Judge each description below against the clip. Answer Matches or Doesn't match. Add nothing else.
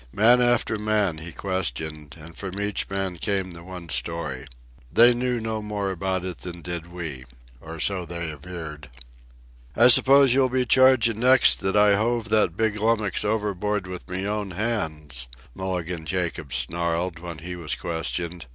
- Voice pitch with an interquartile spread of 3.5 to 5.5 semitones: Matches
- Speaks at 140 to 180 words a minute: Matches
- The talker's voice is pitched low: Matches